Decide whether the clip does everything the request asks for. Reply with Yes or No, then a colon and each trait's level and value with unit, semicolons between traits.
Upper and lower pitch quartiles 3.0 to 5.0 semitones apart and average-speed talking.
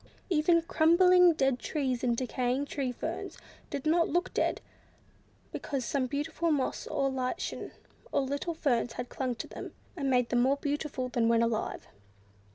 Yes: average, 4.0 semitones; average, 160 wpm